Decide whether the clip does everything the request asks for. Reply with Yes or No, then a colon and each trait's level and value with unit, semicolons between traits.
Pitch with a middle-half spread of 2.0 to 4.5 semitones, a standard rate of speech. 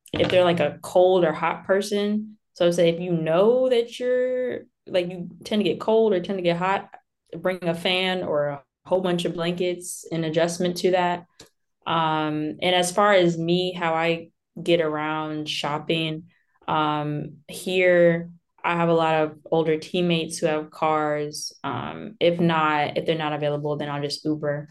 Yes: average, 2.9 semitones; average, 180 wpm